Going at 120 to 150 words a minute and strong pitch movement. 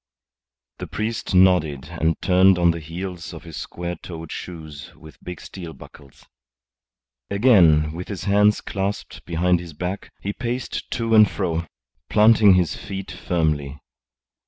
No: average, 140 wpm; average, 3.5 semitones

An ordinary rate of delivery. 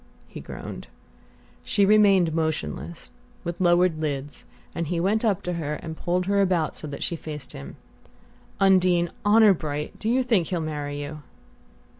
Yes: average, 160 wpm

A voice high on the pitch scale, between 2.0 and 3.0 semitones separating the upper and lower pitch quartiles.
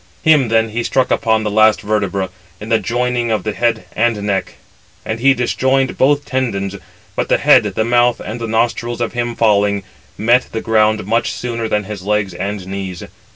No: low, 110 Hz; narrow, 2.4 semitones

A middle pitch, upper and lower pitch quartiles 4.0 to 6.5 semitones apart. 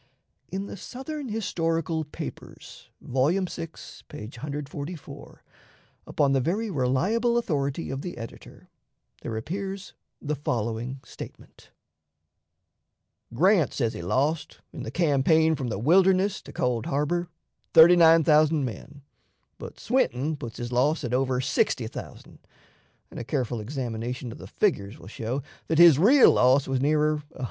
Yes: medium, 150 Hz; average, 5.2 semitones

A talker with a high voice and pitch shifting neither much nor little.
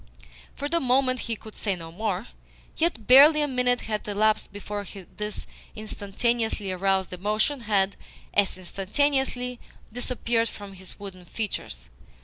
Yes: high, 215 Hz; average, 4.2 semitones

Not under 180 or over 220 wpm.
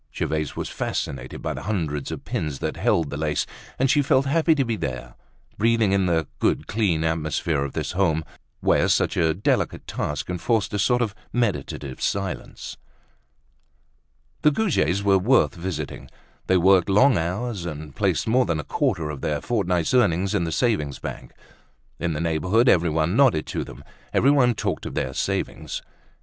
No: average, 170 wpm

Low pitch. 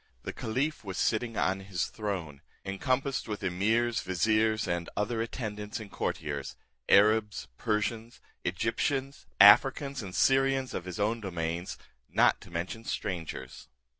Yes: low, 105 Hz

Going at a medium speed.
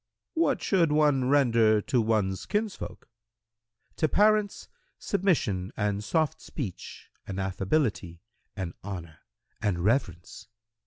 No: slow, 105 wpm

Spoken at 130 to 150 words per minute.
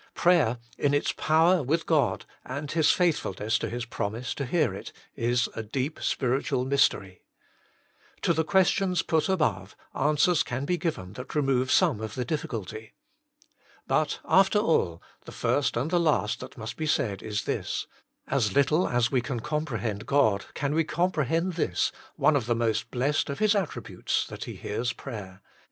No: average, 175 wpm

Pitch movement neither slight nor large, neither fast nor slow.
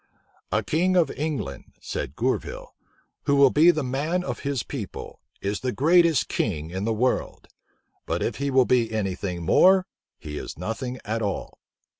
No: wide, 7.0 semitones; average, 170 wpm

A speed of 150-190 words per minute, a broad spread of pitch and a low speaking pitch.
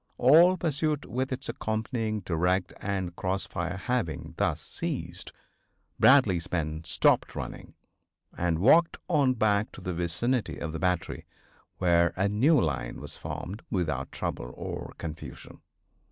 No: slow, 135 wpm; wide, 6.8 semitones; very low, 95 Hz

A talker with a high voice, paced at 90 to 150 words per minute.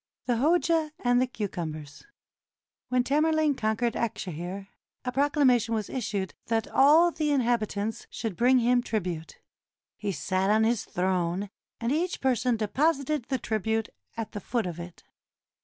Yes: high, 230 Hz; average, 145 wpm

